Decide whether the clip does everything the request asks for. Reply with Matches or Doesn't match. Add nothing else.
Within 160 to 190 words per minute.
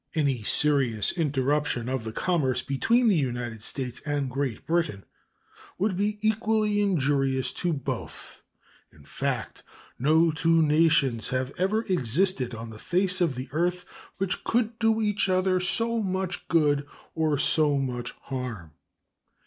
Doesn't match